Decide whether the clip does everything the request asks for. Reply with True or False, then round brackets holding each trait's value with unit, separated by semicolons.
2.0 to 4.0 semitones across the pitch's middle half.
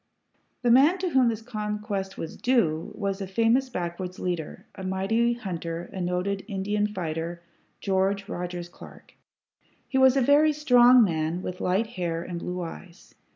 False (5.0 semitones)